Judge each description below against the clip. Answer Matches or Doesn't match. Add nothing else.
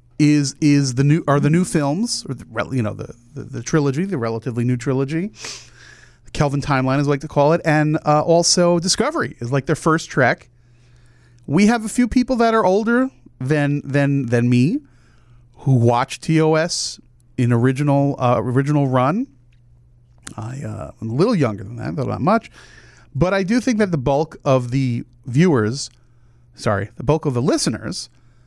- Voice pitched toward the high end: Doesn't match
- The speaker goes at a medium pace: Matches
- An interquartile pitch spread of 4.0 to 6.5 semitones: Matches